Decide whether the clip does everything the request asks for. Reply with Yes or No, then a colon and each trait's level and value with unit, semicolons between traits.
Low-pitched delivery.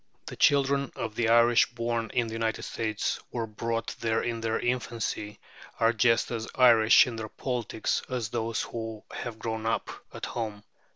Yes: low, 115 Hz